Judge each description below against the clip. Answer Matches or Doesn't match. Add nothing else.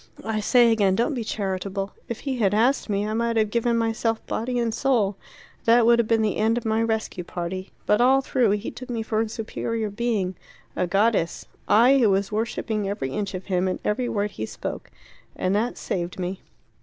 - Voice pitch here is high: Matches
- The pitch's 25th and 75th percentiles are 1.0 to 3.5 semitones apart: Matches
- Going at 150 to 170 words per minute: Doesn't match